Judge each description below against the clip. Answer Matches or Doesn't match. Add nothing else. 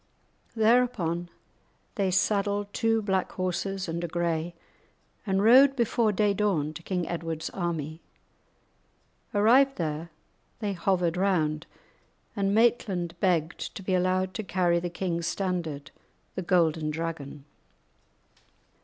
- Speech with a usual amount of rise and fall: Matches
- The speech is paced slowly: Matches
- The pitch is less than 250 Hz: Matches